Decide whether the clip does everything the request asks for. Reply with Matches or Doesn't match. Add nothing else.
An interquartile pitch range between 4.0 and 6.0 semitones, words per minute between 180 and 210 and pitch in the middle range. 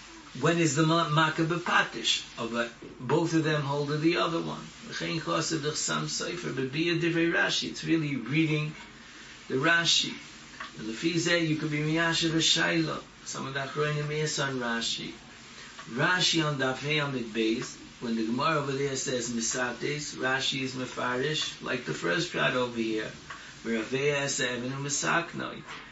Matches